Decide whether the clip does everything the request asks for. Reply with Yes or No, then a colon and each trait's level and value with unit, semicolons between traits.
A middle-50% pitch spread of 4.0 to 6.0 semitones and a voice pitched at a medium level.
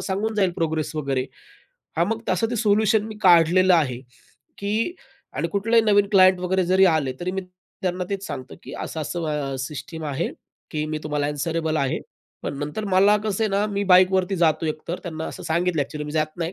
Yes: average, 4.3 semitones; medium, 175 Hz